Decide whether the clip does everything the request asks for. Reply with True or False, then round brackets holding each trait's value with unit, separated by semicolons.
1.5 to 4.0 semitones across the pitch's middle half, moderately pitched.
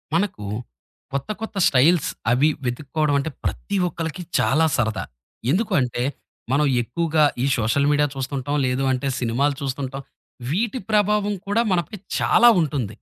False (5.2 semitones; 145 Hz)